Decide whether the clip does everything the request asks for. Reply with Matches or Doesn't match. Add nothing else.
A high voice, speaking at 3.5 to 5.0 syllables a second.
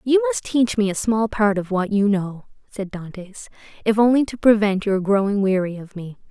Doesn't match